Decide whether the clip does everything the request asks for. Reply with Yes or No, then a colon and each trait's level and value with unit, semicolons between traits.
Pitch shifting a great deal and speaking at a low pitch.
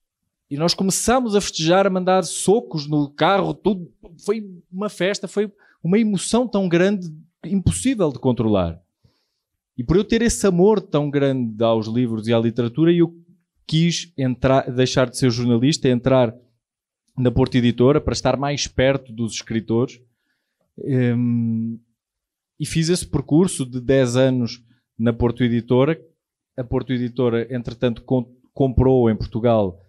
Yes: wide, 6.3 semitones; low, 130 Hz